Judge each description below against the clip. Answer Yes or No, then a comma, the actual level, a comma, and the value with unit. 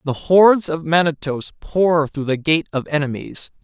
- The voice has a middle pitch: Yes, medium, 155 Hz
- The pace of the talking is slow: No, average, 165 wpm